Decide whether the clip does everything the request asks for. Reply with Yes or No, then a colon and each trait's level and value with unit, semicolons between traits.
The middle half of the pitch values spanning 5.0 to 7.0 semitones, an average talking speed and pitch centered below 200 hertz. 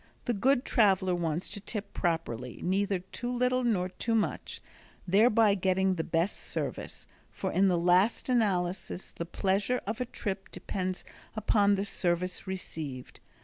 No: average, 3.4 semitones; average, 145 wpm; high, 190 Hz